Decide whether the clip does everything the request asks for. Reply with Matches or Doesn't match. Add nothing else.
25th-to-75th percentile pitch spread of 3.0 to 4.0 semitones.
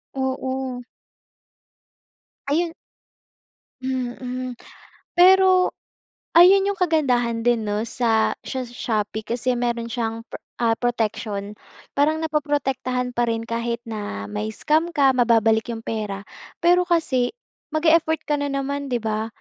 Doesn't match